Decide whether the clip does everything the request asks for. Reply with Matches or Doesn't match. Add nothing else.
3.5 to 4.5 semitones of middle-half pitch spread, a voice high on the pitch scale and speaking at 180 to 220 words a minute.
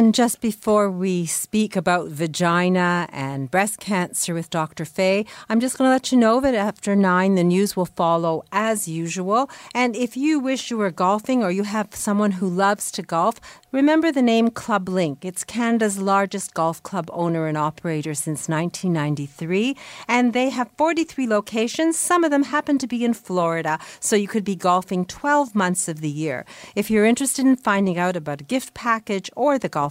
Doesn't match